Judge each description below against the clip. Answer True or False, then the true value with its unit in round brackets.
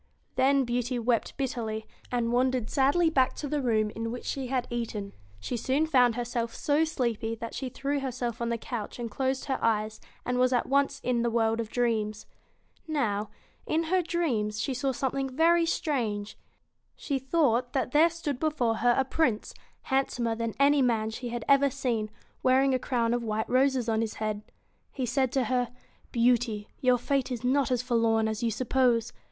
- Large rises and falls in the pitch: False (2.9 semitones)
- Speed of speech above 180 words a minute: True (195 wpm)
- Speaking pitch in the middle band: False (245 Hz)